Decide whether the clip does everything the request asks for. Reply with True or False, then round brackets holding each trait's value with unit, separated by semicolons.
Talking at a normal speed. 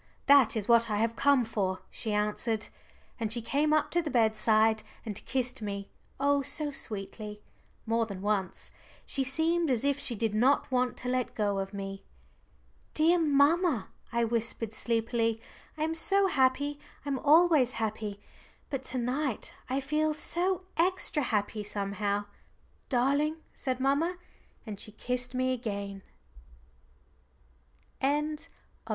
True (145 wpm)